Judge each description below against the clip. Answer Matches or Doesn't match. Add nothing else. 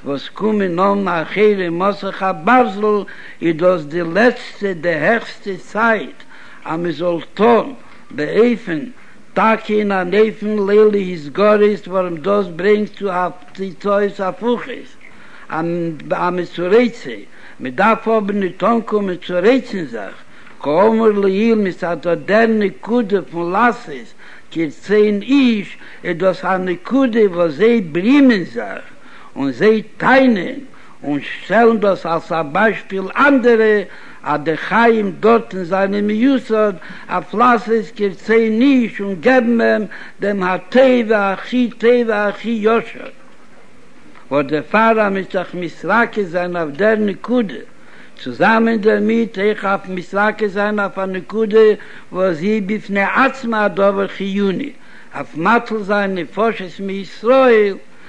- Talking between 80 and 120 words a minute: Doesn't match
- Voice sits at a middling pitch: Doesn't match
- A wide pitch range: Doesn't match